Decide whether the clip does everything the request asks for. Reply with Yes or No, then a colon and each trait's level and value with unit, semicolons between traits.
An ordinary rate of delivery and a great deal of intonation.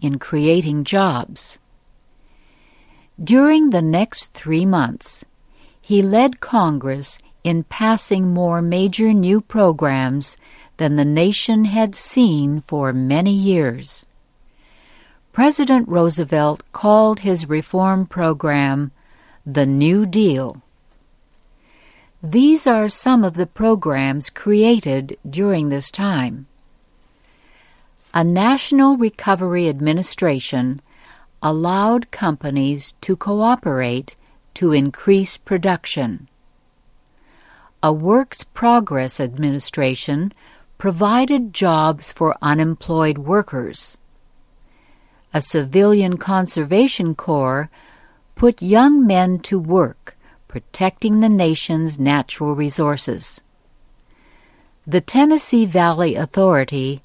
No: slow, 85 wpm; wide, 5.9 semitones